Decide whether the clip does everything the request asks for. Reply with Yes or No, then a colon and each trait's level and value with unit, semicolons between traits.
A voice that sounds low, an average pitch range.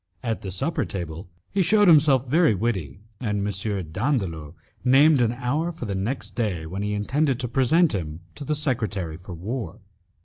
No: low, 115 Hz; wide, 6.6 semitones